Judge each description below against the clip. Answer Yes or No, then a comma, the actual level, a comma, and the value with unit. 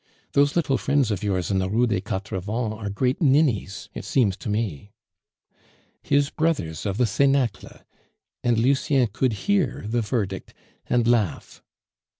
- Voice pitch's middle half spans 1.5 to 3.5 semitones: No, average, 5.1 semitones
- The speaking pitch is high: No, low, 115 Hz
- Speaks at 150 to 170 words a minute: Yes, average, 155 wpm